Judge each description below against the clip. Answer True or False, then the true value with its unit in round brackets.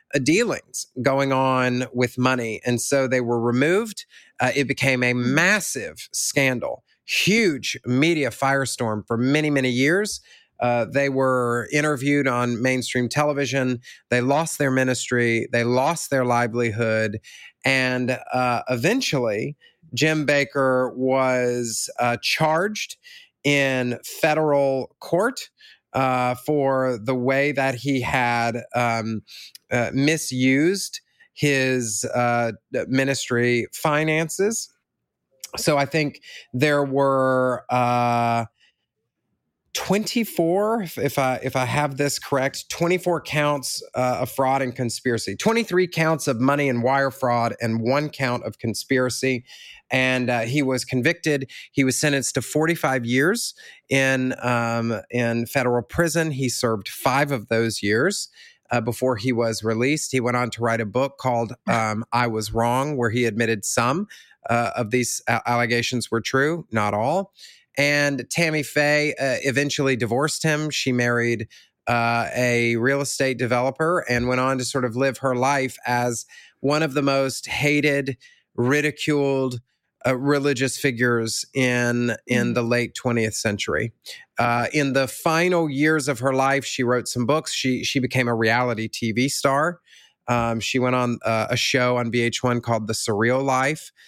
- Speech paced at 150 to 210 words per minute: False (140 wpm)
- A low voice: True (130 Hz)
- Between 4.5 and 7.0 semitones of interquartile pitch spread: False (2.9 semitones)